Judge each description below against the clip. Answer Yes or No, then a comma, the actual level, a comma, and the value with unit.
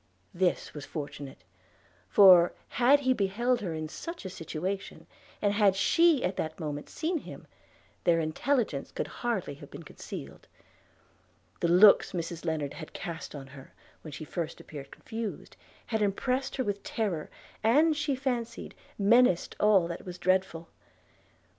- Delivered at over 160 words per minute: No, average, 145 wpm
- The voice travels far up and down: Yes, wide, 6.6 semitones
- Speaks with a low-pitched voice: No, high, 190 Hz